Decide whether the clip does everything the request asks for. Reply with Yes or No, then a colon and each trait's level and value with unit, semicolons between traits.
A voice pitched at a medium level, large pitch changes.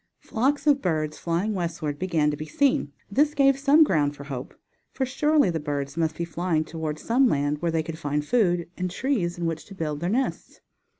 Yes: medium, 170 Hz; wide, 8.2 semitones